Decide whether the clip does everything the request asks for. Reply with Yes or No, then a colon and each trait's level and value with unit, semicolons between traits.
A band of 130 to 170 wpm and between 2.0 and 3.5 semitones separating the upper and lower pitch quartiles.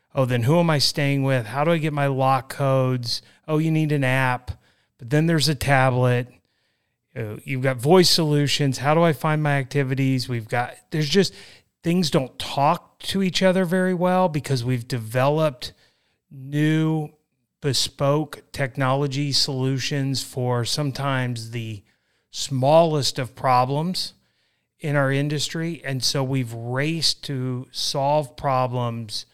Yes: average, 140 wpm; average, 3.2 semitones